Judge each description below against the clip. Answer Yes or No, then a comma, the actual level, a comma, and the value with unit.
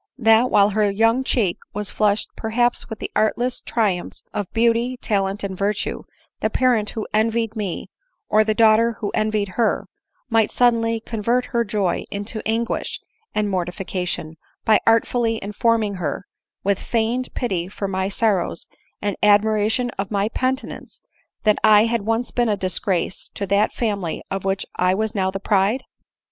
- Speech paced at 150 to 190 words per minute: Yes, average, 155 wpm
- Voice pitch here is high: Yes, high, 215 Hz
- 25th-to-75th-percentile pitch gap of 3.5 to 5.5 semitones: No, narrow, 2.5 semitones